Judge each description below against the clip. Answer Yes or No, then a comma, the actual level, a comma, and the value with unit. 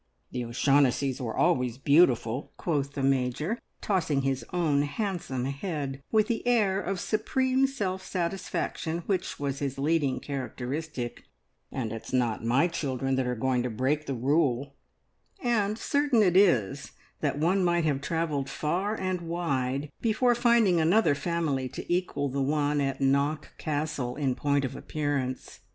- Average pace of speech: Yes, average, 150 wpm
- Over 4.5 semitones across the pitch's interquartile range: Yes, average, 5.1 semitones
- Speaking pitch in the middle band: Yes, medium, 145 Hz